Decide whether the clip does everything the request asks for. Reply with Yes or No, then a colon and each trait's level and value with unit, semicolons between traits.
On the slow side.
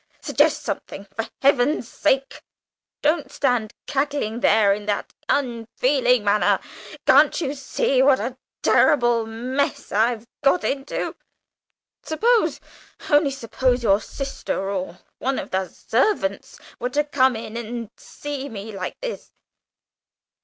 Yes: slow, 125 wpm